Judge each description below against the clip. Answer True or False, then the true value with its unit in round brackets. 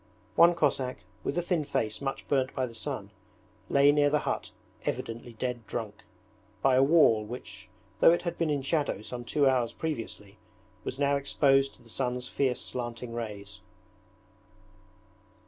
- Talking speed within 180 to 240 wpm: False (160 wpm)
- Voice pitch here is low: True (130 Hz)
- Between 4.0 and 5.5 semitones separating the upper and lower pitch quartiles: False (3.6 semitones)